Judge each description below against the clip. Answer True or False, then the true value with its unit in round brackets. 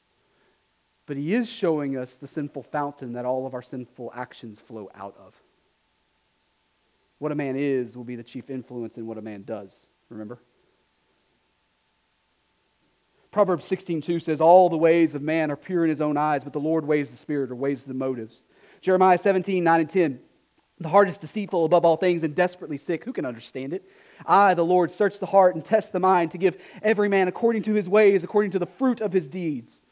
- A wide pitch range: True (6.1 semitones)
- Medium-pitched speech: True (160 Hz)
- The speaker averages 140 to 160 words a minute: False (205 wpm)